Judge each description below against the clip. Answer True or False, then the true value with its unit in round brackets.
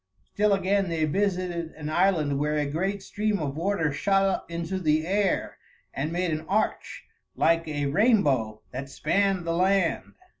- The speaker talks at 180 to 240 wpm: False (160 wpm)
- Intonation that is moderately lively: True (4.3 semitones)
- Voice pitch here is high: False (170 Hz)